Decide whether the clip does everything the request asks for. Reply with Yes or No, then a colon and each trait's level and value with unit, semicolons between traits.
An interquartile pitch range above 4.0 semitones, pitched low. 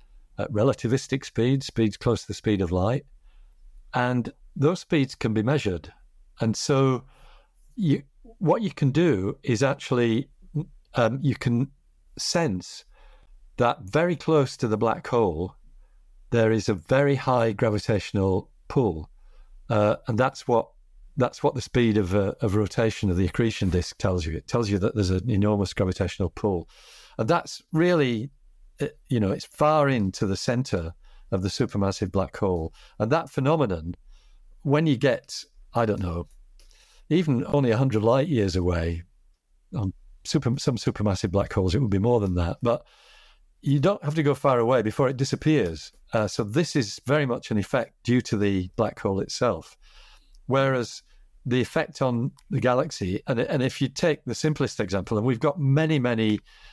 Yes: wide, 5.5 semitones; low, 120 Hz